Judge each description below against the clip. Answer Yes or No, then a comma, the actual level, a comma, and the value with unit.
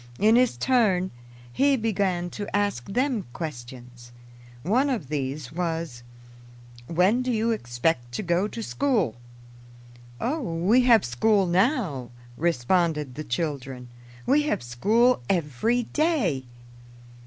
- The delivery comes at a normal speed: No, slow, 120 wpm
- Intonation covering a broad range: Yes, wide, 9.0 semitones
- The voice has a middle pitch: Yes, medium, 180 Hz